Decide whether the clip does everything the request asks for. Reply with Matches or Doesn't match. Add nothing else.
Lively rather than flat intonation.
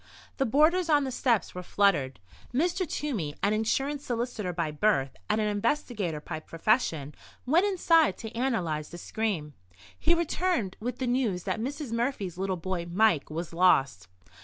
Matches